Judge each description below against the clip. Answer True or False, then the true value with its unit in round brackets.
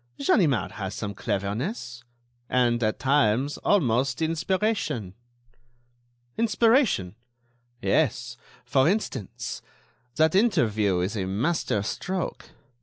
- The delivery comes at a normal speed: False (90 wpm)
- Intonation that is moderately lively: False (8.8 semitones)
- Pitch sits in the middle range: False (125 Hz)